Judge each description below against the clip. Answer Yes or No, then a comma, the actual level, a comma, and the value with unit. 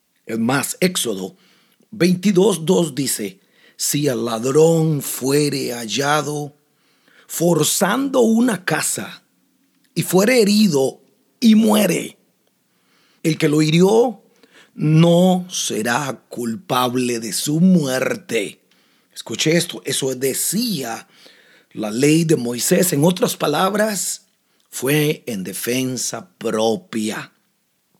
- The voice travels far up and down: Yes, wide, 6.6 semitones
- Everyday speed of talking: No, slow, 90 wpm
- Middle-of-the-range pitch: Yes, medium, 160 Hz